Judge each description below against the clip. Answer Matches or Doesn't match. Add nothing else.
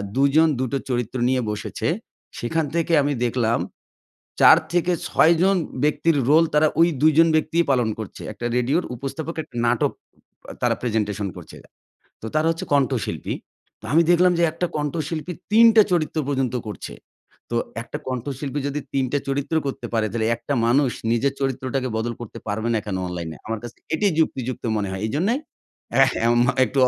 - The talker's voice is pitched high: Doesn't match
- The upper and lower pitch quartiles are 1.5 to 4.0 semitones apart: Doesn't match